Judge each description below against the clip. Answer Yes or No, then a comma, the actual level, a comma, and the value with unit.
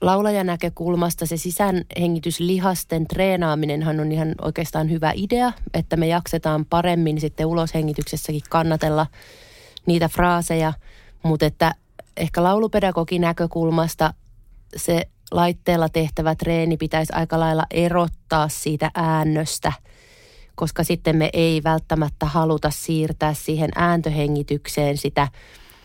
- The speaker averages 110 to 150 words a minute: No, average, 100 wpm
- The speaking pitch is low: No, medium, 160 Hz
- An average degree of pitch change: No, narrow, 1.7 semitones